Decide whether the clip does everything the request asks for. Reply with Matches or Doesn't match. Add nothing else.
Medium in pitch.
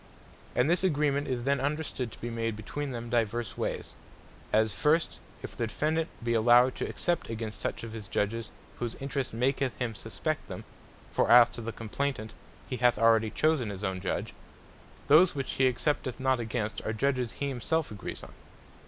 Doesn't match